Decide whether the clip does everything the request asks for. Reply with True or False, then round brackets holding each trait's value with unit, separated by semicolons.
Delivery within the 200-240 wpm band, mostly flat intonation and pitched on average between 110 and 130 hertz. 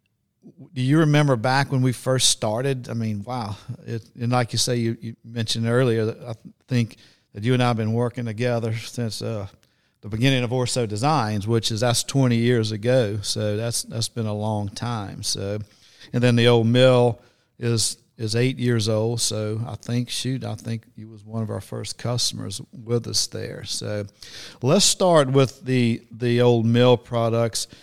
False (190 wpm; 2.0 semitones; 115 Hz)